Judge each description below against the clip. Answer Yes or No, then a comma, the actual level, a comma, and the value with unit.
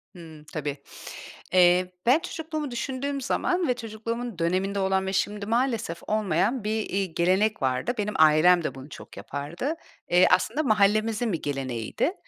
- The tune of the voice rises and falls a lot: Yes, wide, 5.9 semitones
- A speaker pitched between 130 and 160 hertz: No, high, 200 Hz